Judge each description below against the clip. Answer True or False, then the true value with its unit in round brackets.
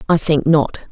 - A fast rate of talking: False (195 wpm)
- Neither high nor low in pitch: True (150 Hz)